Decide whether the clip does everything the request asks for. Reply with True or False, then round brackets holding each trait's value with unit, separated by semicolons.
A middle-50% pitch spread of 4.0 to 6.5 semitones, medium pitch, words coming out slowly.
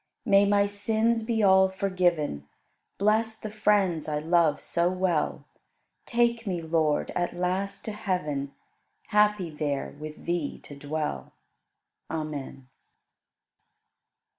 True (5.0 semitones; 180 Hz; 115 wpm)